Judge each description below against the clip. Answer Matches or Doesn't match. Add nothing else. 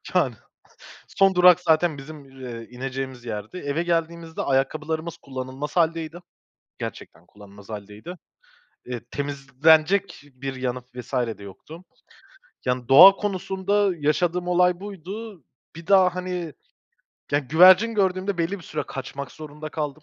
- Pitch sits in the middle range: Matches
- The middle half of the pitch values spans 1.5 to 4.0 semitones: Doesn't match